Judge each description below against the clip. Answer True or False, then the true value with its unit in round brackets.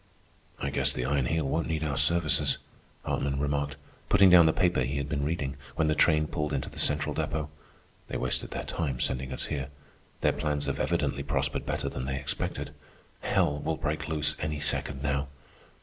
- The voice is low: True (75 Hz)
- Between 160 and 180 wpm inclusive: False (190 wpm)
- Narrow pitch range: True (2.0 semitones)